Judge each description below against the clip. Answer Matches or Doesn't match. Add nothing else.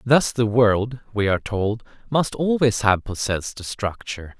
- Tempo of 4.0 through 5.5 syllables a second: Matches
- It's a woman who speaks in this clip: Doesn't match